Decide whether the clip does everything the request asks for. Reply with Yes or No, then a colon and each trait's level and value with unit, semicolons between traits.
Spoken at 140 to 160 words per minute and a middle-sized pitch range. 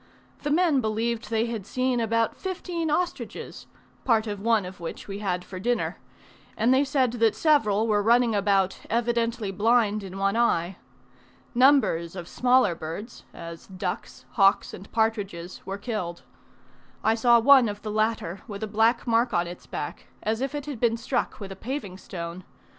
No: average, 170 wpm; average, 3.6 semitones